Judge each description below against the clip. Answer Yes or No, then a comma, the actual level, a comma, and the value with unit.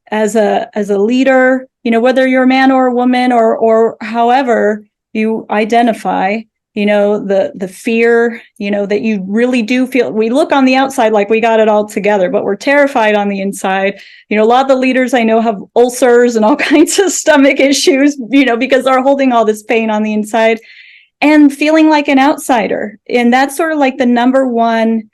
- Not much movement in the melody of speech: No, average, 3.5 semitones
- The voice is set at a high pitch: Yes, high, 235 Hz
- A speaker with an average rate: No, fast, 210 wpm